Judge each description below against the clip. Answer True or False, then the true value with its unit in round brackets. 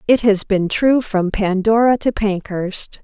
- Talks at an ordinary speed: True (160 wpm)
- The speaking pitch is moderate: False (210 Hz)